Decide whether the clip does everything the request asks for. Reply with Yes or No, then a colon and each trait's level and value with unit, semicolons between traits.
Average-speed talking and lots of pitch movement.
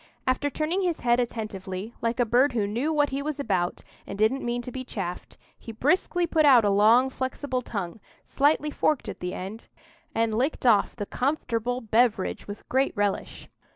No: average, 185 wpm; average, 4.6 semitones